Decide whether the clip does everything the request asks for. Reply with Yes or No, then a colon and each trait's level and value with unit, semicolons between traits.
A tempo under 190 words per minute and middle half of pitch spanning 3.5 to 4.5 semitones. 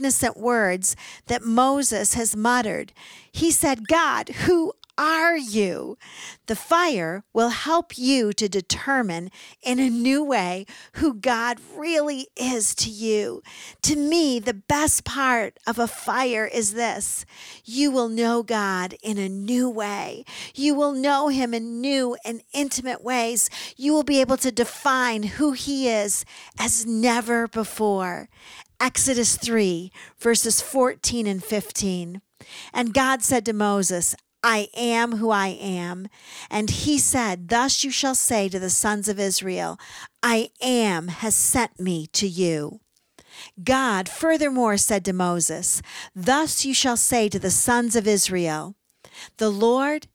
Yes: average, 140 wpm; average, 4.2 semitones